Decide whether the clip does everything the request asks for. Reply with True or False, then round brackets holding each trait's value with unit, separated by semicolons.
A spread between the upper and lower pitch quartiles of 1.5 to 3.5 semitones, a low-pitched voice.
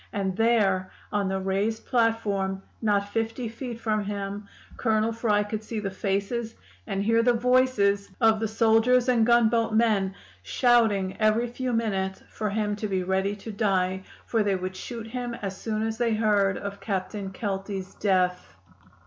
False (2.7 semitones; 215 Hz)